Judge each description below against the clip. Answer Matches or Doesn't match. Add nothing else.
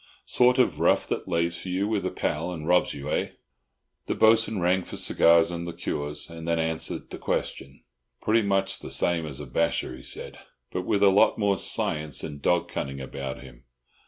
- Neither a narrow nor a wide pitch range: Matches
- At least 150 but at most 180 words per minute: Doesn't match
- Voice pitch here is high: Doesn't match